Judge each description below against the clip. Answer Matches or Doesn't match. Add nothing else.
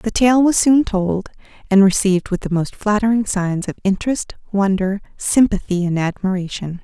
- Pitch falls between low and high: Doesn't match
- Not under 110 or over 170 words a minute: Matches